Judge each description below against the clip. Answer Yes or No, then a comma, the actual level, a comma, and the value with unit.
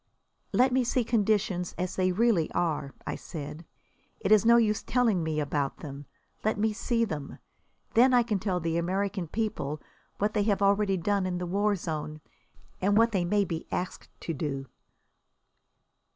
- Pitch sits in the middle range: No, high, 195 Hz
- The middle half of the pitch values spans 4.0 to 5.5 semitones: Yes, average, 4.7 semitones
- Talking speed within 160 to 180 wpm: Yes, average, 170 wpm